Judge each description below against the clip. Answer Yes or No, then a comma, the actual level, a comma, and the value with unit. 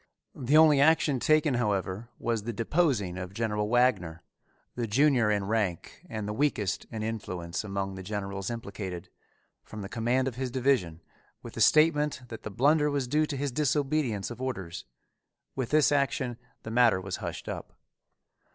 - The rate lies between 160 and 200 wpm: Yes, average, 165 wpm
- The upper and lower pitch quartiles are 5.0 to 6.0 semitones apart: Yes, wide, 5.6 semitones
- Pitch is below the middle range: Yes, low, 115 Hz